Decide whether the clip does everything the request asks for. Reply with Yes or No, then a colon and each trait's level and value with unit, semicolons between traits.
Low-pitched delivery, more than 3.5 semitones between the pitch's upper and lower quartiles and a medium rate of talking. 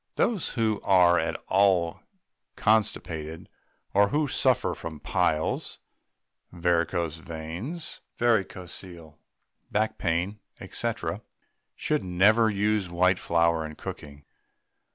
No: very low, 90 Hz; average, 4.2 semitones; slow, 95 wpm